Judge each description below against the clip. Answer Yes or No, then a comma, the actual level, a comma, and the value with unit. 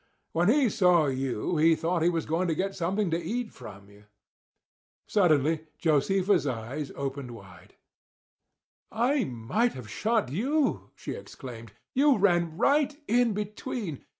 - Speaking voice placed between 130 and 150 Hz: No, medium, 170 Hz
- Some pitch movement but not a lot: No, wide, 7.6 semitones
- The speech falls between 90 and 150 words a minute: Yes, average, 140 wpm